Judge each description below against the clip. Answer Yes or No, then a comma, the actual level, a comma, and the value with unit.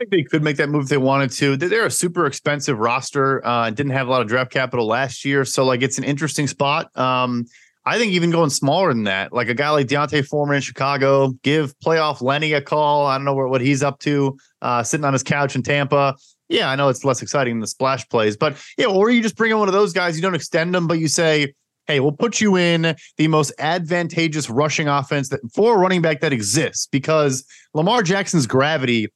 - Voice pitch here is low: No, medium, 145 Hz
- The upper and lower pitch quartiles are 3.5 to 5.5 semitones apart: No, average, 3.0 semitones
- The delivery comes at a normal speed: No, fast, 245 wpm